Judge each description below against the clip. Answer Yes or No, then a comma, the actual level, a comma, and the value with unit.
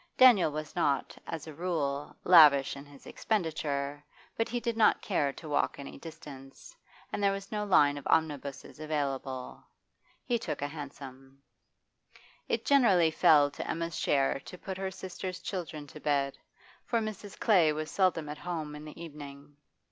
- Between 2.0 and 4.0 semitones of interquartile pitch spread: No, average, 4.4 semitones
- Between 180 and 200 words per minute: No, average, 165 wpm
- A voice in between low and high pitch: Yes, medium, 155 Hz